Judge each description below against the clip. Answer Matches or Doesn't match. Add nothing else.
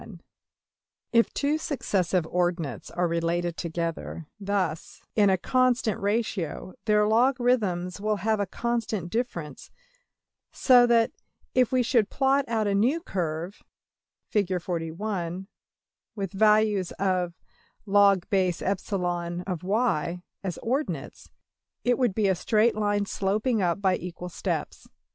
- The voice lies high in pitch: Matches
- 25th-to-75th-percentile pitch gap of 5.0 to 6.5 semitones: Doesn't match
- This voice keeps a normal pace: Doesn't match